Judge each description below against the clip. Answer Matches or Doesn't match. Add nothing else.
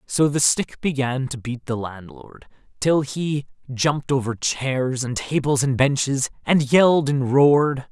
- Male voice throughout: Matches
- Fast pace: Doesn't match